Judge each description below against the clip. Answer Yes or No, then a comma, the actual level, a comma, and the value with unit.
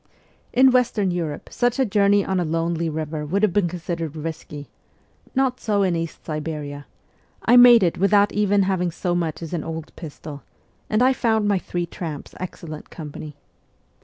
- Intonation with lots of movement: No, average, 4.4 semitones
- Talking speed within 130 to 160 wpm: No, average, 170 wpm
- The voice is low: No, medium, 175 Hz